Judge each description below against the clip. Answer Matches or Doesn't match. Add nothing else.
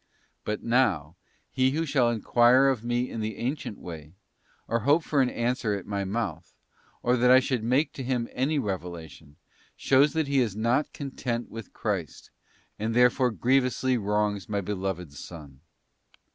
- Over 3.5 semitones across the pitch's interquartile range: Matches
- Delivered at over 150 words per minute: Matches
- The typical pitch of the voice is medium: Doesn't match